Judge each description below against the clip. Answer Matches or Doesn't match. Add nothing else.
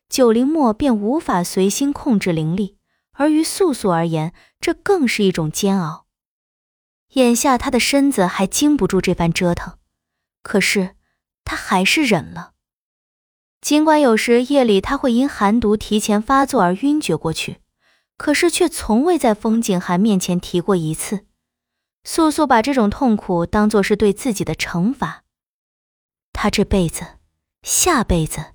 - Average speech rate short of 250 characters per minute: Matches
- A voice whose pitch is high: Matches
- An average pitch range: Doesn't match